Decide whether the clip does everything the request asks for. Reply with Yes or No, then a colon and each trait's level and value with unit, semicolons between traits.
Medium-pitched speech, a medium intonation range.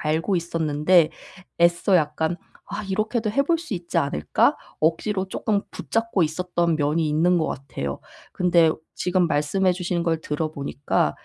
Yes: medium, 170 Hz; average, 3.5 semitones